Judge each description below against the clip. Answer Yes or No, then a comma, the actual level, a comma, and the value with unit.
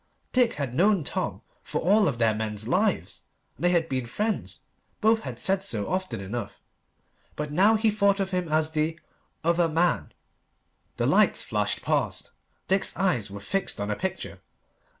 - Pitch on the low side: No, medium, 170 Hz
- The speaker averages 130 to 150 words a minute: No, average, 170 wpm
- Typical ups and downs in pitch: No, wide, 7.7 semitones